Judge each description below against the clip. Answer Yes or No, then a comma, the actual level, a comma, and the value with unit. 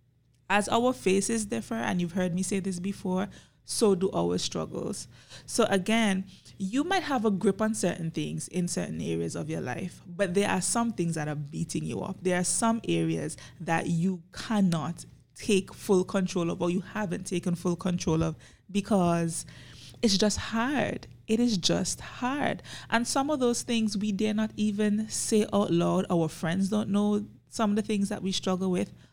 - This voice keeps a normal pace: Yes, average, 185 wpm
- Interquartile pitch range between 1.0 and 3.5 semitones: No, average, 4.0 semitones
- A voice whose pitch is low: No, high, 190 Hz